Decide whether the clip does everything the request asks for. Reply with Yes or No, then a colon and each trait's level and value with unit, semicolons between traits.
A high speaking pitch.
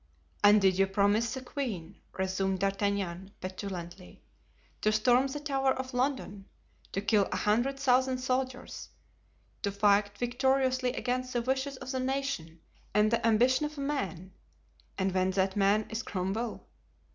Yes: high, 215 Hz